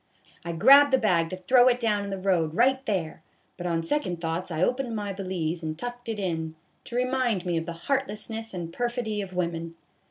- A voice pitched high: Yes, high, 195 Hz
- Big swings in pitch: Yes, wide, 6.2 semitones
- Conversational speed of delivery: No, fast, 210 wpm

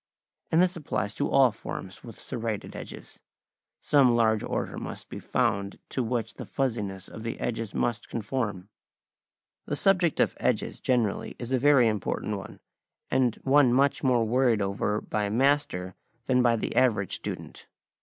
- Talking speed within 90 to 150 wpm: No, average, 160 wpm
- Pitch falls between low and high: No, low, 115 Hz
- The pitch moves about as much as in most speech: Yes, average, 3.9 semitones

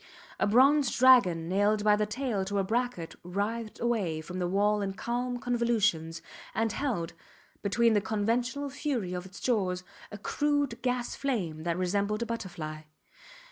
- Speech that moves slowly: No, average, 155 wpm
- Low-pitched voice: No, high, 210 Hz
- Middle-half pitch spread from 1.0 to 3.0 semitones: No, average, 4.7 semitones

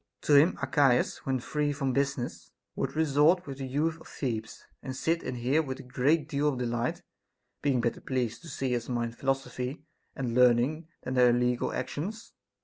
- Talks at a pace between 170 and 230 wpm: Yes, average, 180 wpm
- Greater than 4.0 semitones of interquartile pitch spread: No, average, 3.1 semitones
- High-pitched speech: No, low, 135 Hz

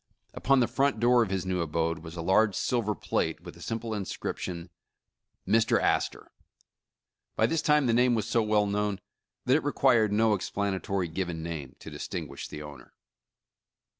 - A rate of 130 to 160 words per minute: No, average, 170 wpm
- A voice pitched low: Yes, low, 105 Hz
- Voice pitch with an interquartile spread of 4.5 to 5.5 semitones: Yes, average, 5.0 semitones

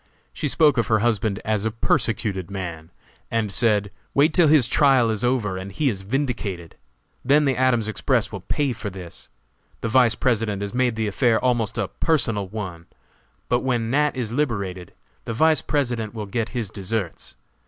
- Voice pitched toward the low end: Yes, low, 115 Hz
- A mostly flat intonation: No, average, 4.0 semitones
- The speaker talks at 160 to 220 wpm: Yes, average, 175 wpm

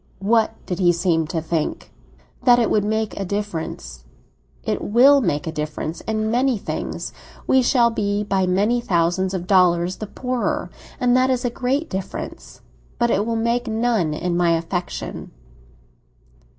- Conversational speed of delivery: Yes, average, 155 wpm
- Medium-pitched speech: No, high, 205 Hz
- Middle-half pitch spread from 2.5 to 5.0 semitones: No, wide, 5.4 semitones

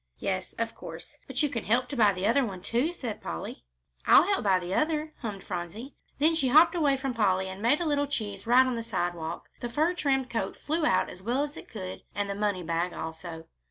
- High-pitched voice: Yes, high, 230 Hz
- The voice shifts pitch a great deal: Yes, wide, 7.1 semitones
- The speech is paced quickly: Yes, fast, 230 wpm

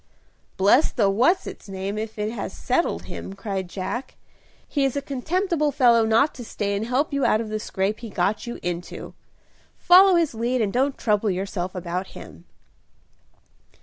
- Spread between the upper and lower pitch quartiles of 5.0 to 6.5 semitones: Yes, wide, 5.6 semitones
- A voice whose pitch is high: Yes, high, 220 Hz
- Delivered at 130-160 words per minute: No, average, 175 wpm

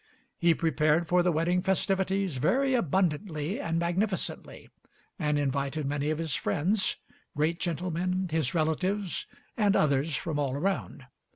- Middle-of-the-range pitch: Yes, medium, 165 Hz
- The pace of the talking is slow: Yes, slow, 130 wpm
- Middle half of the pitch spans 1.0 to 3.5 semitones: No, average, 3.9 semitones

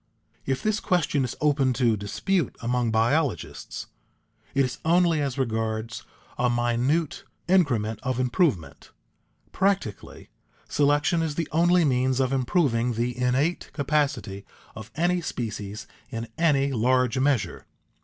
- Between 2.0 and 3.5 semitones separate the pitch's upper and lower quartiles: No, average, 4.7 semitones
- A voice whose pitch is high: No, low, 130 Hz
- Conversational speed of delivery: No, slow, 125 wpm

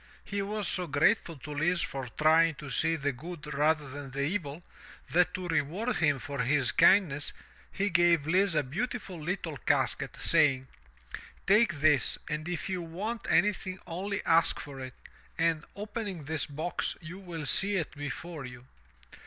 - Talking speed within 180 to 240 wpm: No, average, 160 wpm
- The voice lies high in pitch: No, medium, 165 Hz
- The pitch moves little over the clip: No, average, 4.2 semitones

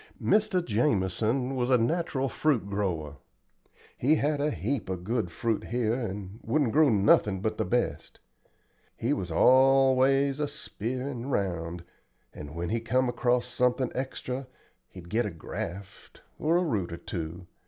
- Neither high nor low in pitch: No, low, 120 Hz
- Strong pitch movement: Yes, wide, 5.8 semitones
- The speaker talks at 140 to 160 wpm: Yes, average, 150 wpm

